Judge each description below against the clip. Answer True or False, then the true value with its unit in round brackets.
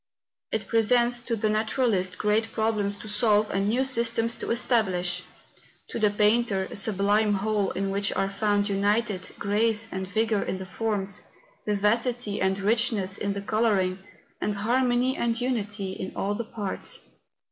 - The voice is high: True (210 Hz)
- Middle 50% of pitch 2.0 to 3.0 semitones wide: True (2.5 semitones)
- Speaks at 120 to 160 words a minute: True (155 wpm)